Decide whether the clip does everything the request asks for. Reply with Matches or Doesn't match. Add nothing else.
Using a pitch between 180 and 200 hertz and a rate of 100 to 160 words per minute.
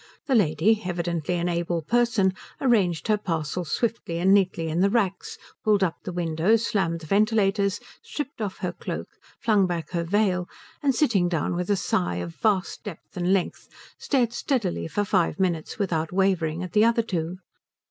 Doesn't match